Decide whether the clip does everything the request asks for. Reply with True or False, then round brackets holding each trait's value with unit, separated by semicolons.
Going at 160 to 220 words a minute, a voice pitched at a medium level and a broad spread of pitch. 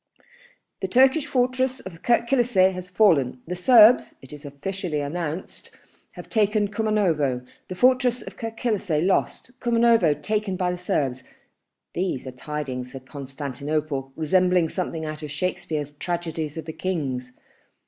False (140 wpm; 175 Hz; 6.4 semitones)